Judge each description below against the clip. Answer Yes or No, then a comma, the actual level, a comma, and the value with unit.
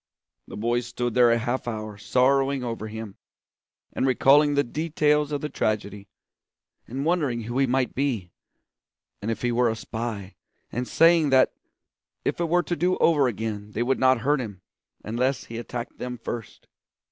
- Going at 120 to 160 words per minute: No, average, 170 wpm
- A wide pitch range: No, average, 3.7 semitones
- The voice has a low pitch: Yes, low, 125 Hz